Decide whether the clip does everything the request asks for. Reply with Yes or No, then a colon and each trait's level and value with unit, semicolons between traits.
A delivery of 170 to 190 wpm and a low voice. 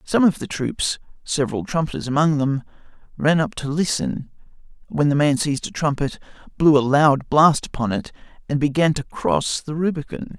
No: average, 175 wpm; medium, 145 Hz